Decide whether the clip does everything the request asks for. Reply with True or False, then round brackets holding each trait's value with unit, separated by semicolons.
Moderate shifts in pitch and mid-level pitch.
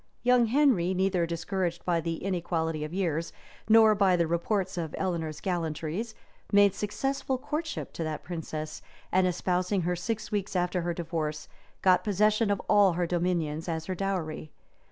True (3.5 semitones; 180 Hz)